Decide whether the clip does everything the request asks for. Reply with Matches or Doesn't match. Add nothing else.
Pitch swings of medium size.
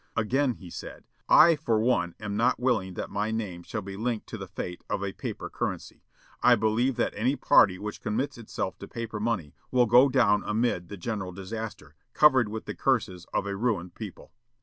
Matches